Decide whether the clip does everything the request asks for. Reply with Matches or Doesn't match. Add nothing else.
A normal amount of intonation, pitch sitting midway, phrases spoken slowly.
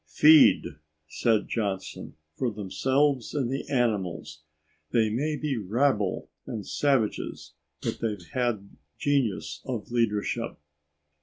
Doesn't match